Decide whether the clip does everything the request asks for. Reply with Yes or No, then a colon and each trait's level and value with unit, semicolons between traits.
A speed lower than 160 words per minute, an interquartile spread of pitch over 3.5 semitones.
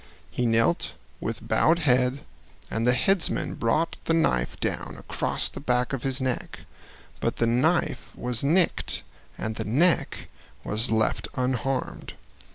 Yes: average, 140 wpm; average, 4.3 semitones